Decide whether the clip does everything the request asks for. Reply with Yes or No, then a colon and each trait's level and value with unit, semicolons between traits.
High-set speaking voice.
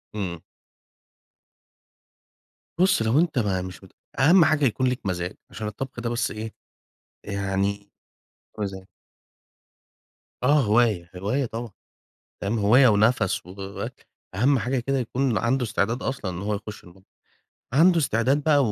No: low, 110 Hz